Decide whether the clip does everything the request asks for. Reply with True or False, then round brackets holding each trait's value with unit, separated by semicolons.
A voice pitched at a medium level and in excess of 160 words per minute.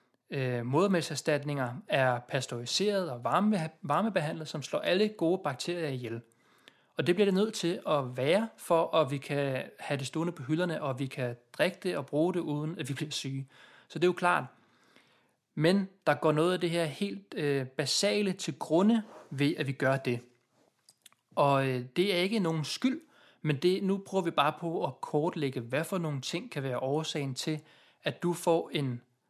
True (155 Hz; 180 wpm)